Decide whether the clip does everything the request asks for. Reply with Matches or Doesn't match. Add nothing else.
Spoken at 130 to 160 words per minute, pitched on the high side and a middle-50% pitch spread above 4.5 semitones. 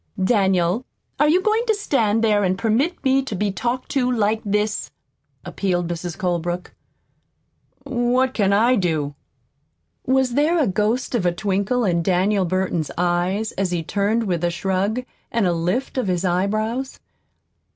Matches